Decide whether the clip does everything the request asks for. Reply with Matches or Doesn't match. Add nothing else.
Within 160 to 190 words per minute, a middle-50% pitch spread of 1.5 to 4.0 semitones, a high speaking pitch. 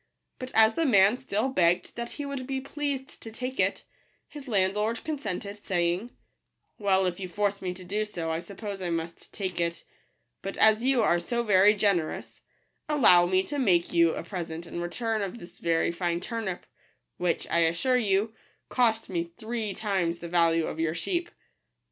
Doesn't match